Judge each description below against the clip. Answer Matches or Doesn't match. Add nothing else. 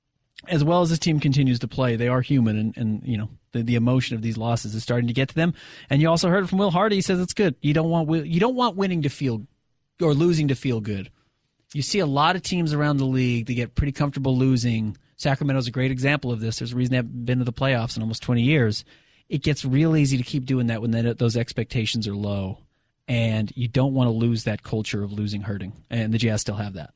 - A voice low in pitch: Matches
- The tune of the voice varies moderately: Matches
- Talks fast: Matches